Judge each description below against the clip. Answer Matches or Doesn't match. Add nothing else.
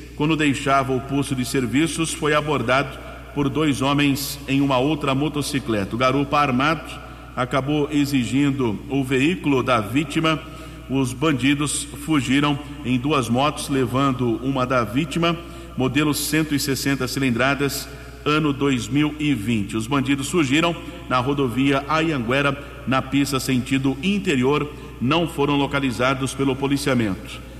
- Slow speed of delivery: Matches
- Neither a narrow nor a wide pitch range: Doesn't match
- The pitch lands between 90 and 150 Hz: Matches